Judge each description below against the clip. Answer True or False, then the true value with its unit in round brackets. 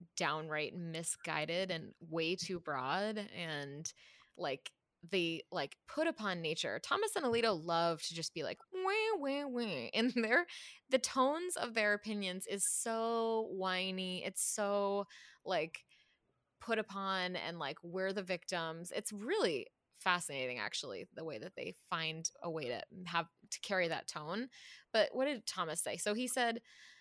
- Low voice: False (190 Hz)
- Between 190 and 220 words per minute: False (155 wpm)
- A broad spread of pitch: True (5.7 semitones)